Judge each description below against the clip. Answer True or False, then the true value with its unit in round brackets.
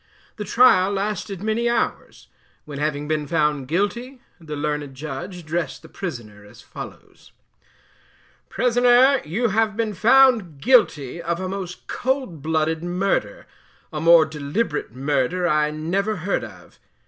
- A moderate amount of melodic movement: False (6.2 semitones)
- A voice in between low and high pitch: True (175 Hz)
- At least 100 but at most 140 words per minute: True (135 wpm)